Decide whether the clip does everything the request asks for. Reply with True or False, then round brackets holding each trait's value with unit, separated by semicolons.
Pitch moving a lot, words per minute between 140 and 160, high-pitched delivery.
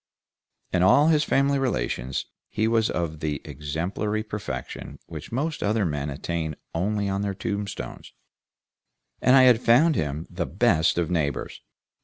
False (6.8 semitones; 145 wpm; 100 Hz)